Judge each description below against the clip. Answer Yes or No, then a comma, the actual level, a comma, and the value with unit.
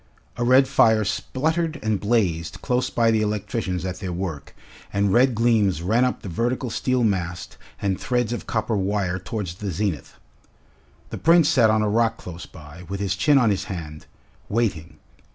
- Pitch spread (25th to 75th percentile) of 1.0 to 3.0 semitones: No, average, 4.5 semitones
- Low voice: Yes, low, 105 Hz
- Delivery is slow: No, average, 175 wpm